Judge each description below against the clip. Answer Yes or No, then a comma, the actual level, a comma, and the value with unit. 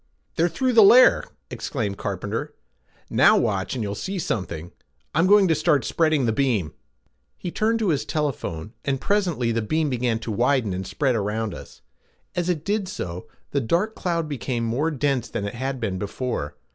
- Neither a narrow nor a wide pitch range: No, wide, 7.1 semitones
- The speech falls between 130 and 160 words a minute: No, average, 180 wpm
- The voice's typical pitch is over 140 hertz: No, low, 135 Hz